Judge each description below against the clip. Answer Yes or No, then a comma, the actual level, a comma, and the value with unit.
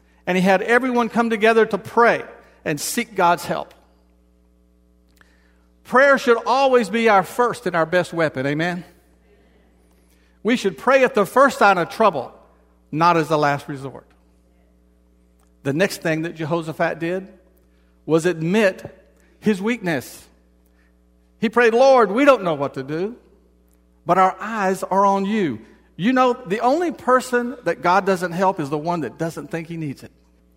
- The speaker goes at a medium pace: Yes, average, 155 wpm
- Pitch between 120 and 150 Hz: No, medium, 170 Hz